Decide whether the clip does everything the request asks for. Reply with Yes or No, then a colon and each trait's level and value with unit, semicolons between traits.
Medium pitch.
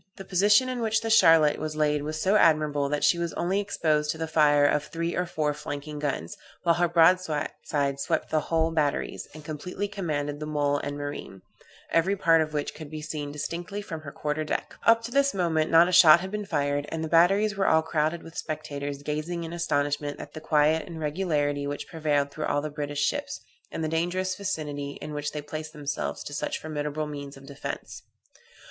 Yes: medium, 155 Hz